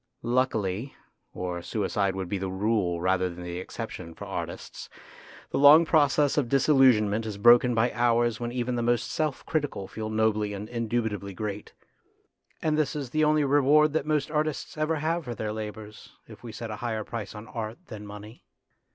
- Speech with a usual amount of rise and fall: Yes, average, 4.9 semitones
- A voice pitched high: No, low, 115 Hz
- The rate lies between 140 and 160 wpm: No, average, 180 wpm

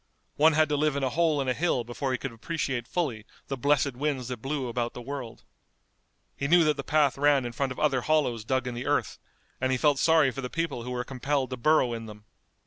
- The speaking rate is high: Yes, fast, 245 wpm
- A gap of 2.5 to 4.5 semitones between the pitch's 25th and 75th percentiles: Yes, average, 3.2 semitones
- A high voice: No, low, 135 Hz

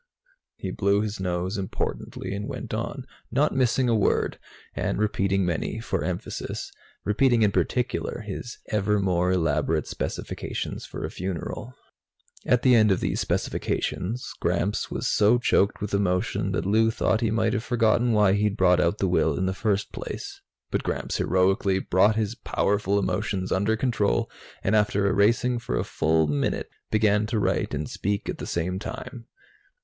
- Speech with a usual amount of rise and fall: Yes, average, 3.0 semitones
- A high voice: No, low, 100 Hz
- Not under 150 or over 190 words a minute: Yes, average, 165 wpm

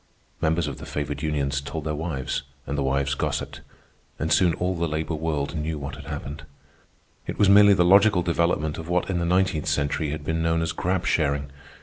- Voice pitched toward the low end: Yes, very low, 80 Hz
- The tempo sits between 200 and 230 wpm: Yes, fast, 205 wpm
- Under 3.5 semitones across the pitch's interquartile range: Yes, average, 3.1 semitones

